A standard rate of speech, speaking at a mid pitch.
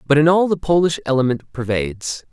Yes: average, 180 wpm; medium, 145 Hz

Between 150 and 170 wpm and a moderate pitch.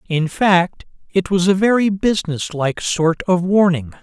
Yes: average, 165 wpm; medium, 180 Hz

